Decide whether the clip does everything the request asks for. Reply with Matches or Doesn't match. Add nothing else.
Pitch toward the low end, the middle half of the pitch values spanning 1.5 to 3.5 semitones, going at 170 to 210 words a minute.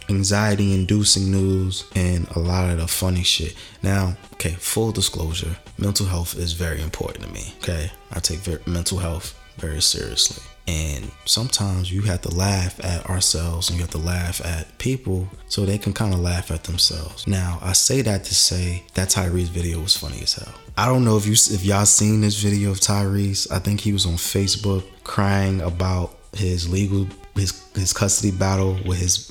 Matches